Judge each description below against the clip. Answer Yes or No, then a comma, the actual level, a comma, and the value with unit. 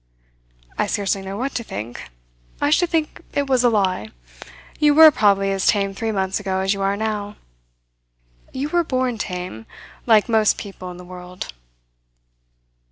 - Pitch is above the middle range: Yes, high, 205 Hz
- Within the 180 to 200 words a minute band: No, average, 165 wpm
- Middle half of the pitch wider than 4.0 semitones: Yes, average, 4.7 semitones